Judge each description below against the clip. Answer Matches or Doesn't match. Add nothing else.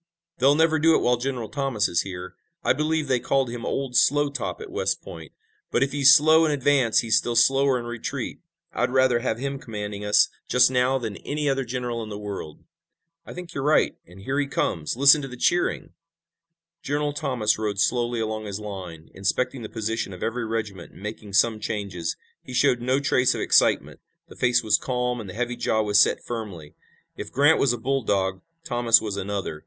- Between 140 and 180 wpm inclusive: Doesn't match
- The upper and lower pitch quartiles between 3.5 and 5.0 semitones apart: Matches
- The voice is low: Matches